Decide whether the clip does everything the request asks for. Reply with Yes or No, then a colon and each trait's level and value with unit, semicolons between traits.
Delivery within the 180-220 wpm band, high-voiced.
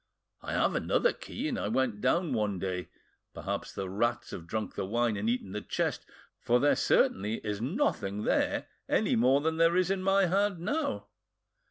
No: average, 185 wpm; low, 125 Hz